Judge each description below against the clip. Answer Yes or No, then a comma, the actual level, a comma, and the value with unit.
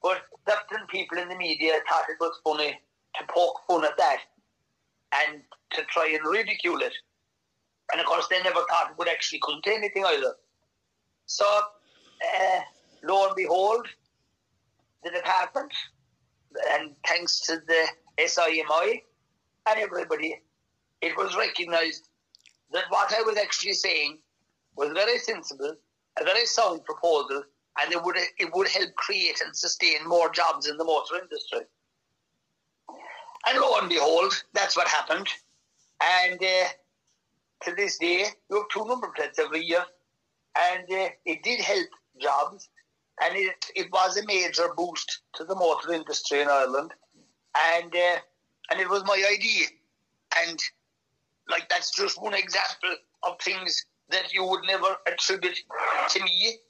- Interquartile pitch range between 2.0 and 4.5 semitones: No, wide, 5.5 semitones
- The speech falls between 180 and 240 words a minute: No, average, 145 wpm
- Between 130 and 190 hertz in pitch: Yes, medium, 185 Hz